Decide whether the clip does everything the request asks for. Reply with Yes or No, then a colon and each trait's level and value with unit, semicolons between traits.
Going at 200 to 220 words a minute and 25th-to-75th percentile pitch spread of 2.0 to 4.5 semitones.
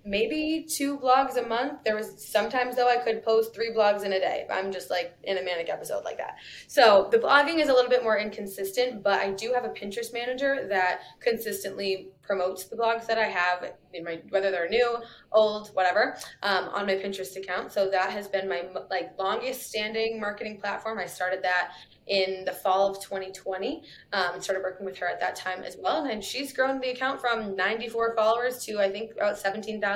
Yes: fast, 205 wpm; average, 3.7 semitones